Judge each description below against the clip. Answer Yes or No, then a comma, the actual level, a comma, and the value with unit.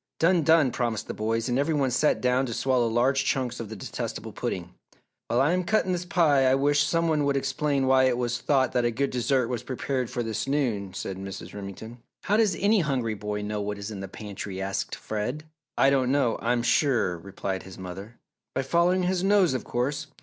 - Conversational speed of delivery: No, fast, 215 wpm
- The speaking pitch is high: No, low, 130 Hz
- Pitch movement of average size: Yes, average, 4.8 semitones